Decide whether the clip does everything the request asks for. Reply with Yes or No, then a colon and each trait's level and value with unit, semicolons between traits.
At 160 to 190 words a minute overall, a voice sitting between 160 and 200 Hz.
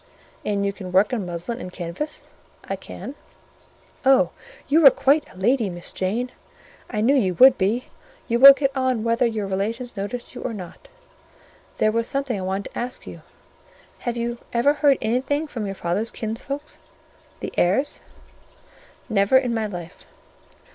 No: average, 165 wpm; high, 230 Hz